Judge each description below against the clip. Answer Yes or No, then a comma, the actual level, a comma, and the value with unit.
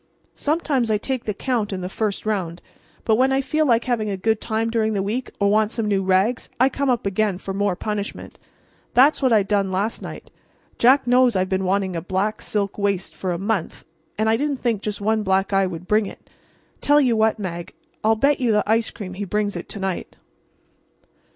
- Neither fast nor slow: No, fast, 215 wpm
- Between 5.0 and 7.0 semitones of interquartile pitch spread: No, average, 3.3 semitones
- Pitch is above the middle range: Yes, high, 210 Hz